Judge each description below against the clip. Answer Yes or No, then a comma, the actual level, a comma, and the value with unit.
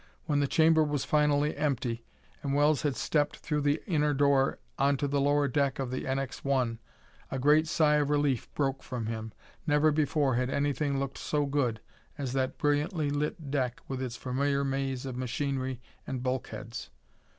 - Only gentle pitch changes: Yes, narrow, 2.0 semitones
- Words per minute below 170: No, average, 175 wpm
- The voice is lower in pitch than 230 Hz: Yes, medium, 140 Hz